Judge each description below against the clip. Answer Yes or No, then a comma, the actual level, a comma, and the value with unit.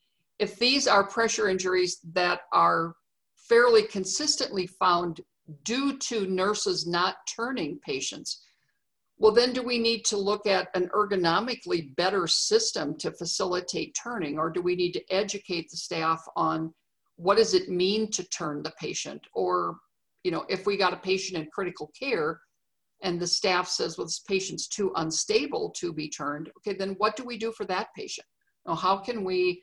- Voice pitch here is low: No, high, 190 Hz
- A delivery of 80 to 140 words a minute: No, average, 170 wpm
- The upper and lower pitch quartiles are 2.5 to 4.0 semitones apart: No, average, 4.4 semitones